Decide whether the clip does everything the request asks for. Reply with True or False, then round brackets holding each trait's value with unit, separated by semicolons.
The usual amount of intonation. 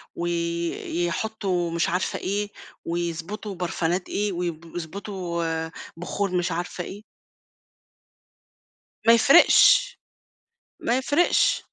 True (3.2 semitones)